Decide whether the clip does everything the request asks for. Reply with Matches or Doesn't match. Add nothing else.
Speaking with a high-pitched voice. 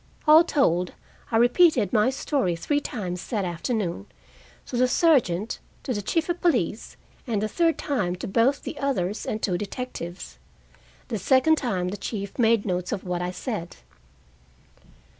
Matches